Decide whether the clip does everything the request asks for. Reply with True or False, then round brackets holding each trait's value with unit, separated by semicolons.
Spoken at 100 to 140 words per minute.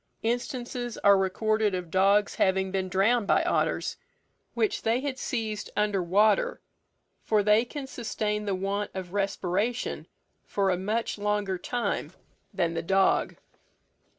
True (135 wpm)